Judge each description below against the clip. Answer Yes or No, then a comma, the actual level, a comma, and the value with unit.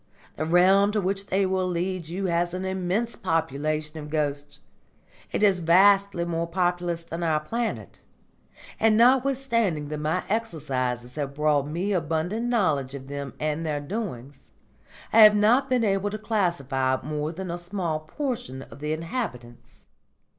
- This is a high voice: No, medium, 170 Hz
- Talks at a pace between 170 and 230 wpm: No, average, 155 wpm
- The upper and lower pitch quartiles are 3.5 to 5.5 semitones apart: Yes, average, 4.9 semitones